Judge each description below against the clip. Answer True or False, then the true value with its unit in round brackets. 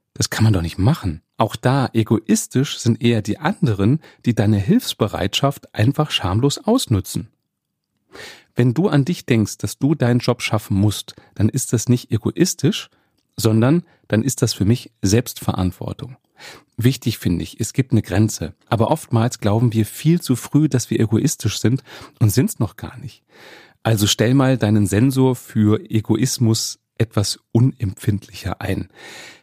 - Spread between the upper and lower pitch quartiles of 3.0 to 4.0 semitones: True (3.7 semitones)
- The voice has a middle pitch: False (115 Hz)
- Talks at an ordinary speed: True (155 wpm)